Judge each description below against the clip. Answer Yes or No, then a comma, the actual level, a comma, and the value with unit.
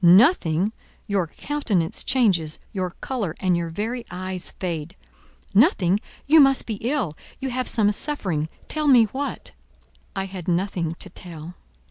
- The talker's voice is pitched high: Yes, high, 195 Hz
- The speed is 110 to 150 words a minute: Yes, average, 140 wpm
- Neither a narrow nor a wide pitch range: No, wide, 6.3 semitones